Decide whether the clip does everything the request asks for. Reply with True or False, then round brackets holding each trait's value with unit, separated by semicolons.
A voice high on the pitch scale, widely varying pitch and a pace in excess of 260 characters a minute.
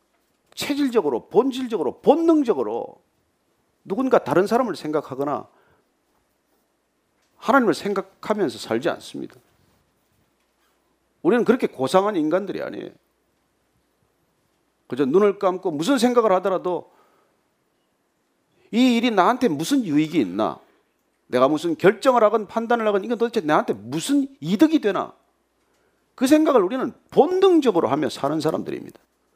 True (235 Hz; 6.5 semitones; 285 characters per minute)